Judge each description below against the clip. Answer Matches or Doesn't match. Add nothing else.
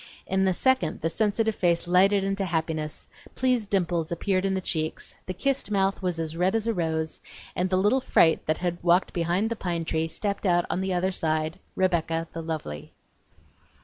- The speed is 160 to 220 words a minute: Matches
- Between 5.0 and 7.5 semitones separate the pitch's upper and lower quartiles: Doesn't match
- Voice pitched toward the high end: Doesn't match